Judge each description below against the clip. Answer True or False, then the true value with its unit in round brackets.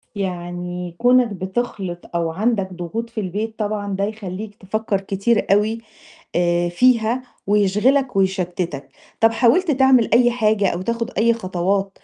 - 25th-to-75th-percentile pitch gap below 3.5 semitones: False (4.0 semitones)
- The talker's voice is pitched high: True (205 Hz)